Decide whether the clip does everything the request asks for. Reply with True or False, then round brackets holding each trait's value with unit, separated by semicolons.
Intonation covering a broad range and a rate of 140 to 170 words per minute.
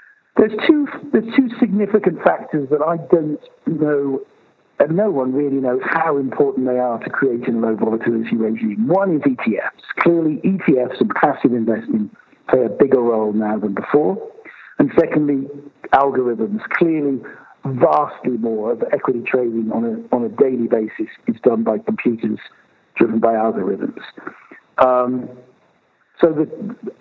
True (8.0 semitones; 145 wpm)